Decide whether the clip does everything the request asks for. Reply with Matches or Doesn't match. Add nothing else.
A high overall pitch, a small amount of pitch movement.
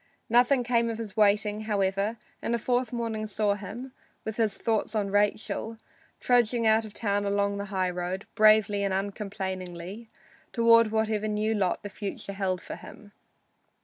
Matches